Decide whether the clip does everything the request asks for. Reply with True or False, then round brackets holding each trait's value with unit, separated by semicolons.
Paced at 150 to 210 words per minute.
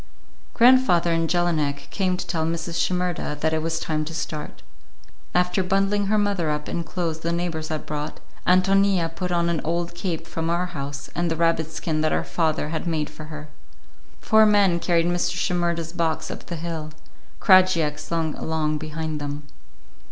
True (175 wpm)